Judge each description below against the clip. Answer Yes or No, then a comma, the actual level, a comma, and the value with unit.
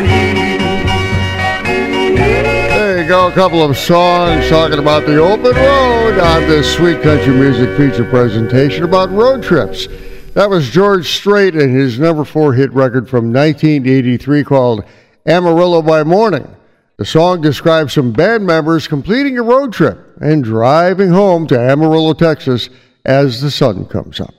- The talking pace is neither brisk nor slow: Yes, average, 145 wpm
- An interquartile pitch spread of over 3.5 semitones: Yes, wide, 5.5 semitones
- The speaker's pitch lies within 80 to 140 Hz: No, medium, 150 Hz